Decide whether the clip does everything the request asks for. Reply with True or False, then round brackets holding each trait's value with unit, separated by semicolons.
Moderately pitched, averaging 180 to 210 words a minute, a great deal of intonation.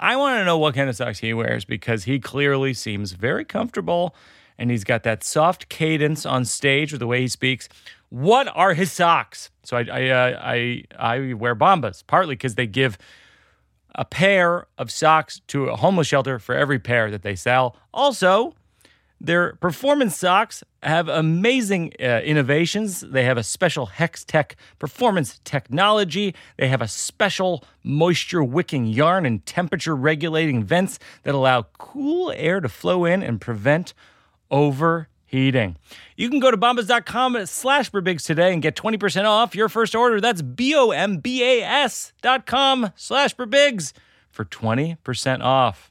False (155 Hz; 150 wpm; 7.5 semitones)